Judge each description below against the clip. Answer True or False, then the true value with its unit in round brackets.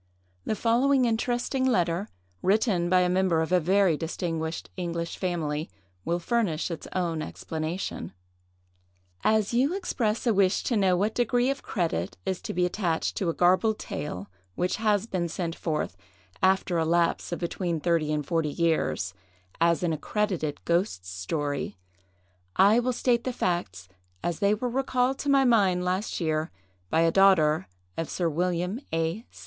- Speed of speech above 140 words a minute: True (160 wpm)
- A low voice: False (180 Hz)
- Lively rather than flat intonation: False (4.7 semitones)